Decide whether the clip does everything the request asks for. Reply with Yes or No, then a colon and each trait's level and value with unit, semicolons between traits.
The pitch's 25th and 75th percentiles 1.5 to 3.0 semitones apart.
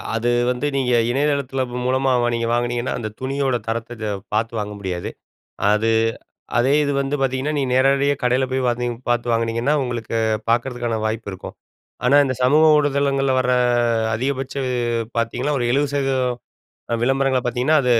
Yes: narrow, 2.4 semitones